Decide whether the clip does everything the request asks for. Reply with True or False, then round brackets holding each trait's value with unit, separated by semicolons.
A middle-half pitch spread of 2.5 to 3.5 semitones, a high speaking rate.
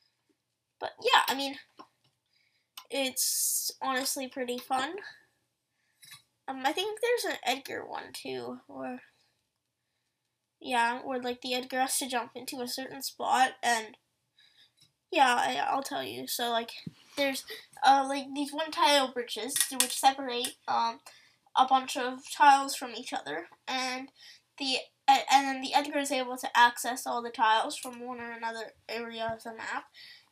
False (2.8 semitones; 150 wpm)